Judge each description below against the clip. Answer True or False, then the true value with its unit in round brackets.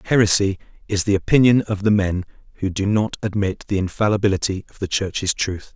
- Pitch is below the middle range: True (100 Hz)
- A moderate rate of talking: True (175 wpm)